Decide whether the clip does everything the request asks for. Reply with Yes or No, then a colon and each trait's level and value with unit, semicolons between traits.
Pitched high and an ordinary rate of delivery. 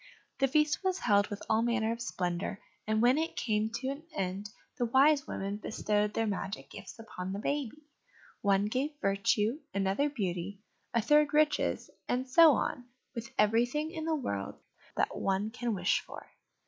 Yes: high, 225 Hz; average, 170 wpm